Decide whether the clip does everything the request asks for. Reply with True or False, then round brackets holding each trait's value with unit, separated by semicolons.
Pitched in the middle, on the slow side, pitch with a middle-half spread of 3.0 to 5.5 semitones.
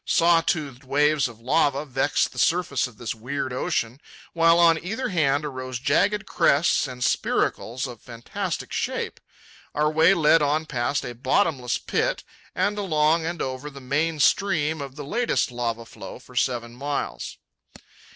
False (145 Hz; 155 wpm; 4.3 semitones)